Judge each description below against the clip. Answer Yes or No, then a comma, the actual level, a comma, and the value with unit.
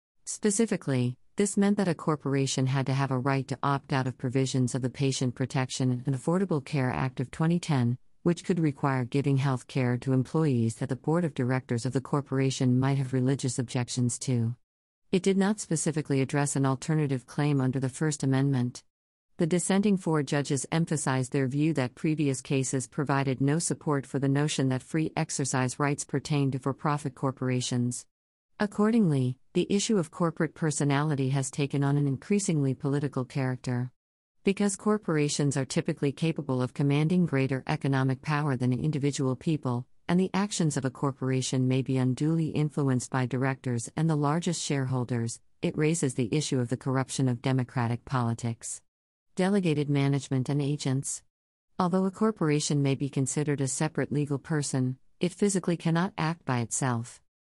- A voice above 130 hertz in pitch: Yes, medium, 140 Hz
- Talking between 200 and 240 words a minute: No, average, 165 wpm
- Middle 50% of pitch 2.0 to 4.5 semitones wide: Yes, average, 3.3 semitones